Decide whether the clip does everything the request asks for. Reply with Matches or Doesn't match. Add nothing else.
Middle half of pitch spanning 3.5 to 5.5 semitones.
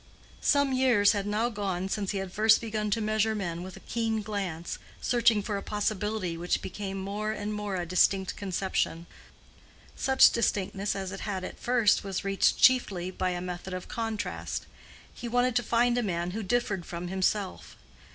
Doesn't match